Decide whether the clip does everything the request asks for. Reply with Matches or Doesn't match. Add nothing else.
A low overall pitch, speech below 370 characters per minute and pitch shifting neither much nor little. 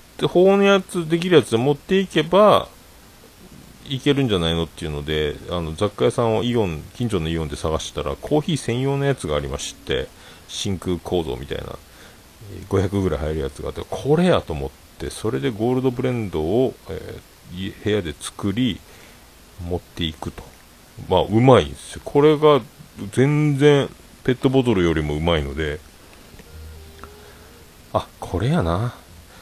Doesn't match